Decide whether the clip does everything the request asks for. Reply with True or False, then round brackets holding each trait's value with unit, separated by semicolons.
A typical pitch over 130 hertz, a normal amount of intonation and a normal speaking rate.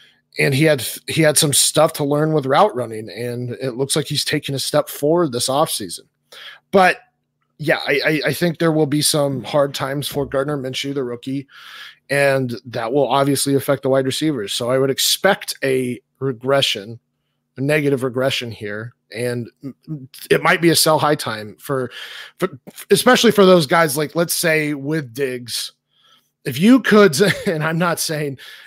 True (140 Hz; 3.2 semitones; 175 wpm)